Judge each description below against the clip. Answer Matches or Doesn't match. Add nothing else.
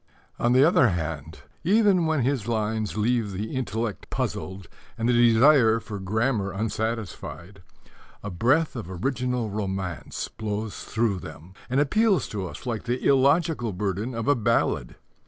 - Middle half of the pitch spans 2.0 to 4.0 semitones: Doesn't match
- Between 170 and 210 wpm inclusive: Doesn't match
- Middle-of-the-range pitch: Doesn't match